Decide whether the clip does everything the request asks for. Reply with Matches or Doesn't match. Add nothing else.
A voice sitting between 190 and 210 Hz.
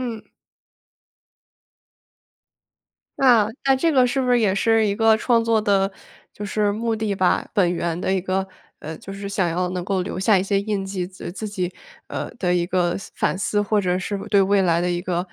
Matches